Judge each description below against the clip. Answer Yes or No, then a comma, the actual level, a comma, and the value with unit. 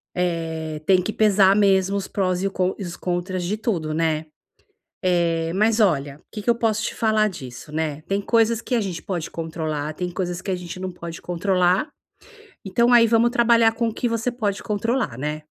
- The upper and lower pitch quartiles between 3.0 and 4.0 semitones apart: No, average, 4.5 semitones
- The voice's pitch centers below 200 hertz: Yes, medium, 185 Hz